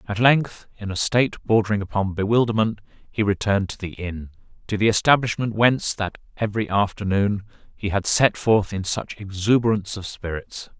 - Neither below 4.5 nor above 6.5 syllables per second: Yes, 5.5 syllables/s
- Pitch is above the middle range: No, low, 105 Hz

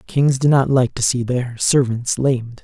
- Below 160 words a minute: No, fast, 205 wpm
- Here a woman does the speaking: No, male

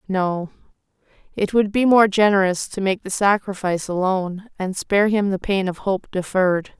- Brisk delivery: No, average, 170 wpm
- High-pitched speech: Yes, high, 195 Hz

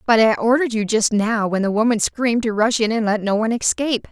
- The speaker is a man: No, female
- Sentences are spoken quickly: Yes, fast, 265 wpm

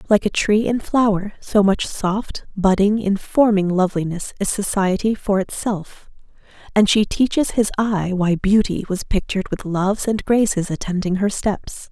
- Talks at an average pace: Yes, average, 155 wpm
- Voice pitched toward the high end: Yes, high, 200 Hz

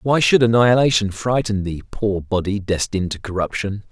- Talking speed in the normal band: Yes, average, 155 wpm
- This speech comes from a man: Yes, male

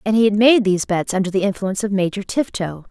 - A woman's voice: Yes, female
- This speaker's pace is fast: Yes, fast, 250 wpm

